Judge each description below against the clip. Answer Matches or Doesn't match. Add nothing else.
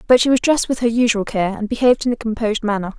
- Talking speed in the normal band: Doesn't match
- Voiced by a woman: Matches